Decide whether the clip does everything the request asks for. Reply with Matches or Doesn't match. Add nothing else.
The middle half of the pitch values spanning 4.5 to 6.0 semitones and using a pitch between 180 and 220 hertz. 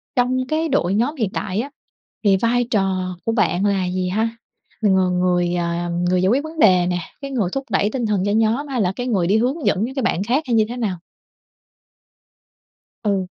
Matches